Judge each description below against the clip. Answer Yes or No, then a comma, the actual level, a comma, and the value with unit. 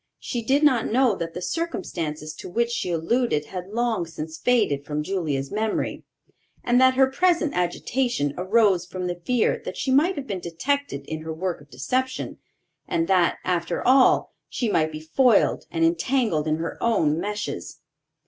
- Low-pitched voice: No, high, 190 Hz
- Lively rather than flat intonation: Yes, wide, 7.5 semitones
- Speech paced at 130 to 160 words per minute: No, average, 170 wpm